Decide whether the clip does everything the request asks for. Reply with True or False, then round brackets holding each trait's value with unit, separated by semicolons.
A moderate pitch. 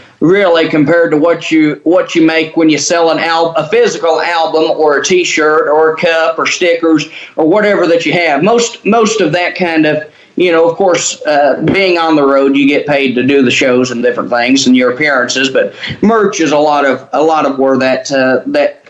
True (160 Hz)